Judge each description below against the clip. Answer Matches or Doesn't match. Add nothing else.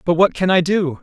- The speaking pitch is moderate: Matches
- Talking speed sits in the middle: Doesn't match